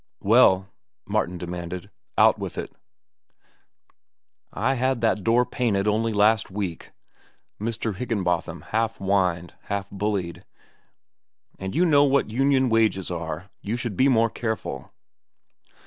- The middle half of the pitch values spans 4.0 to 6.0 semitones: No, average, 3.6 semitones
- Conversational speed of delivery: No, slow, 120 wpm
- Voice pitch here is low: Yes, low, 105 Hz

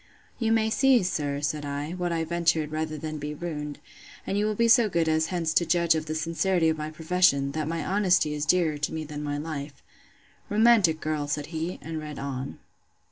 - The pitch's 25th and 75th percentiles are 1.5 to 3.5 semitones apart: Yes, average, 3.0 semitones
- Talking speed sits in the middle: No, fast, 210 wpm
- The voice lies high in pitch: No, medium, 160 Hz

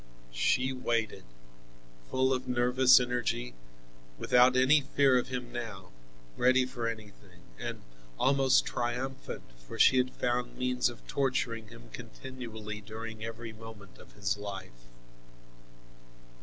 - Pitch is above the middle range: No, low, 120 Hz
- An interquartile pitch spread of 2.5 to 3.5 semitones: Yes, average, 2.8 semitones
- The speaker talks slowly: Yes, slow, 120 wpm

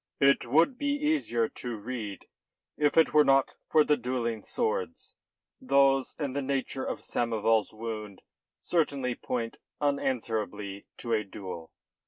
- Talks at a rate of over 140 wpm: No, slow, 135 wpm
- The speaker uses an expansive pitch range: No, average, 4.6 semitones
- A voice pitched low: Yes, low, 125 Hz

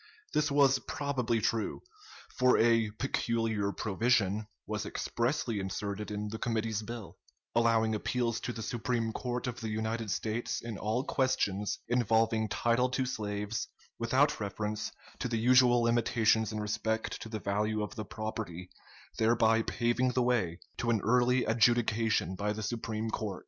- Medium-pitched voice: No, low, 115 Hz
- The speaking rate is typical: Yes, average, 150 wpm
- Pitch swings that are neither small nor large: No, narrow, 2.1 semitones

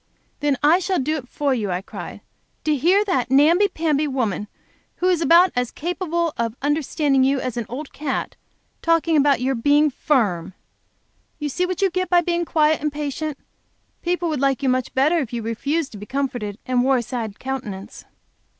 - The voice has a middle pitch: No, very high, 285 Hz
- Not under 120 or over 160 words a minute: No, average, 190 wpm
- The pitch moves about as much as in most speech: Yes, average, 4.5 semitones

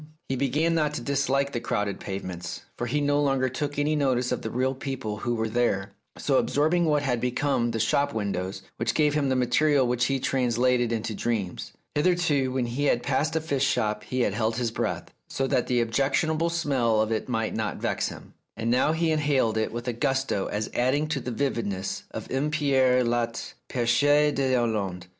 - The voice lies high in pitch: No, low, 125 Hz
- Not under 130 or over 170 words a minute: No, average, 195 wpm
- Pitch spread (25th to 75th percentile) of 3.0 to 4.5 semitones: Yes, average, 3.7 semitones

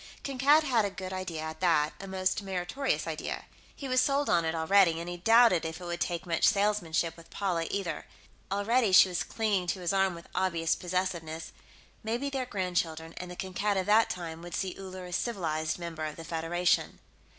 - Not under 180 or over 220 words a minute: Yes, average, 195 wpm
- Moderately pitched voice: Yes, medium, 180 Hz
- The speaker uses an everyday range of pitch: Yes, average, 3.3 semitones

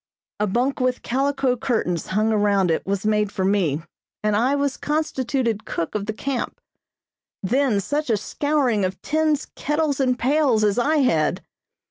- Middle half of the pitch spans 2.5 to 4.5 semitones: No, average, 5.3 semitones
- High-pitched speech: Yes, high, 240 Hz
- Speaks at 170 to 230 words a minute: No, average, 160 wpm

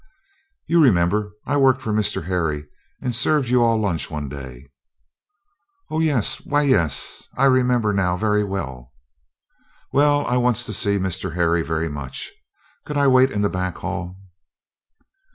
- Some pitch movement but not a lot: No, wide, 6.9 semitones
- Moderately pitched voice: No, low, 105 Hz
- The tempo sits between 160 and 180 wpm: No, average, 150 wpm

